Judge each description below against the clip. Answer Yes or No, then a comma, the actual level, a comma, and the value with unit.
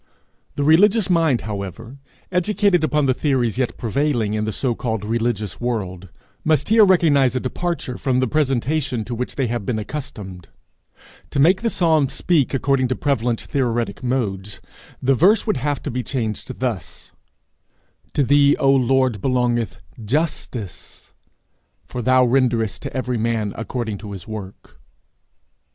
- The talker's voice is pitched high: No, low, 125 Hz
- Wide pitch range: No, average, 4.2 semitones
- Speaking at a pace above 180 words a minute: No, average, 150 wpm